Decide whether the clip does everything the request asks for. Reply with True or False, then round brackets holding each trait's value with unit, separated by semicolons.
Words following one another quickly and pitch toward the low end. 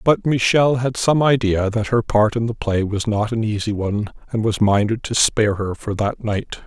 True (225 wpm; 110 Hz)